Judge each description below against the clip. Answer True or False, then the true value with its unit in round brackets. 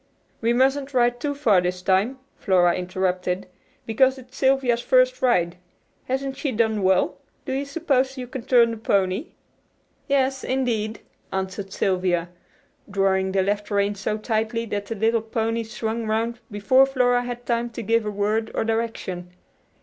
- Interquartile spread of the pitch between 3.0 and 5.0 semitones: True (4.5 semitones)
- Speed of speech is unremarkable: True (155 wpm)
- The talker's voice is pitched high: True (225 Hz)